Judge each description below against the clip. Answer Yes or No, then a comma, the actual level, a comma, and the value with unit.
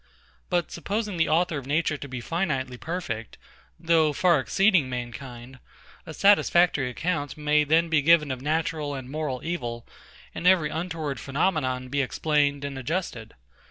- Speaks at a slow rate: No, average, 150 wpm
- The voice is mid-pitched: Yes, medium, 150 Hz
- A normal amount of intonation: Yes, average, 4.2 semitones